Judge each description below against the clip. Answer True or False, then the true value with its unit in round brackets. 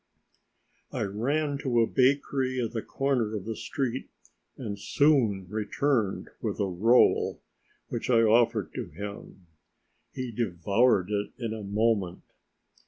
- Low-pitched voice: True (115 Hz)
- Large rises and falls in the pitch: False (3.9 semitones)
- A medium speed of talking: False (125 wpm)